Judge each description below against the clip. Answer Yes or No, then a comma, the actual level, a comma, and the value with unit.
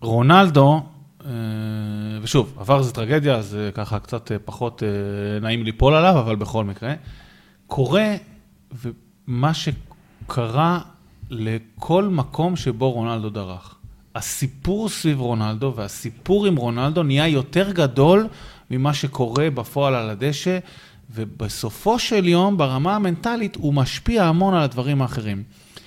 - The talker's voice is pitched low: Yes, low, 130 Hz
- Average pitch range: No, wide, 6.4 semitones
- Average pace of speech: Yes, average, 110 wpm